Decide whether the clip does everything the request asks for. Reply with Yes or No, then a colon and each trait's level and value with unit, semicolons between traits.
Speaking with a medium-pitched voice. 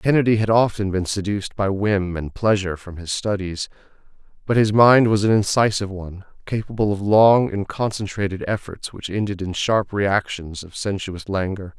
No: low, 100 Hz